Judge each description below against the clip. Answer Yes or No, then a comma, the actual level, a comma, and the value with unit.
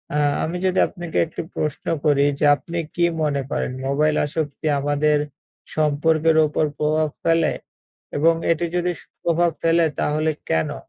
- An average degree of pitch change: No, narrow, 1.9 semitones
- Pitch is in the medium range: Yes, medium, 155 Hz